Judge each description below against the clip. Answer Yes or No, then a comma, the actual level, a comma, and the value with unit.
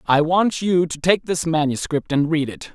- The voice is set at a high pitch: No, medium, 160 Hz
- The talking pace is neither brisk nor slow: No, fast, 220 wpm